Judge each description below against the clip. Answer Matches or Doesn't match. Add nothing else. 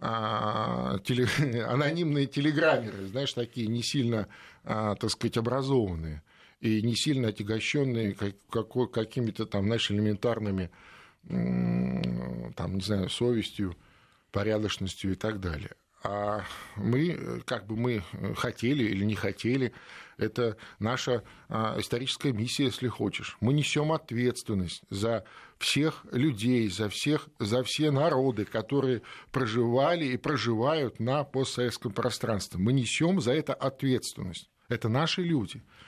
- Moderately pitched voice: Doesn't match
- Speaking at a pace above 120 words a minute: Doesn't match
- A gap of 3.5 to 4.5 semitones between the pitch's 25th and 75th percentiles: Matches